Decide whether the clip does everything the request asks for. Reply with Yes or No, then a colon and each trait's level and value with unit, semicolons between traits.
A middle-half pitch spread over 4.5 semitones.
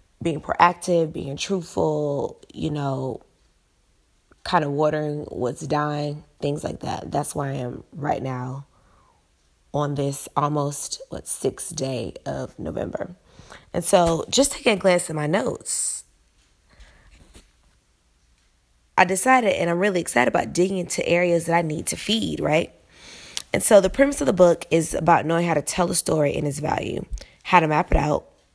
Yes: average, 4.9 semitones